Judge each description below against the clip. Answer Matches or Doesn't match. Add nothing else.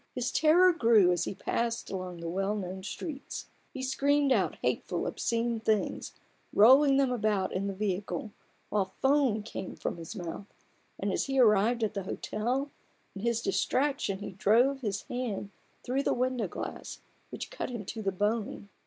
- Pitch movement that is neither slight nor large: Matches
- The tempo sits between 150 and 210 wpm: Matches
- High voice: Matches